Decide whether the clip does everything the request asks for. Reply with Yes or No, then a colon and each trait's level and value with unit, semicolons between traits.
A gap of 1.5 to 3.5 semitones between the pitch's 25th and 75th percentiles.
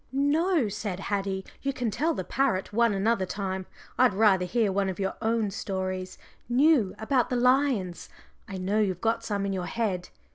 No: average, 4.3 semitones